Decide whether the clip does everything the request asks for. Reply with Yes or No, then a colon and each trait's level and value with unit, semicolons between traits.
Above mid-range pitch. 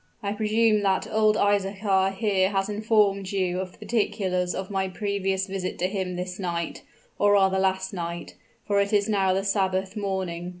Yes: high, 195 Hz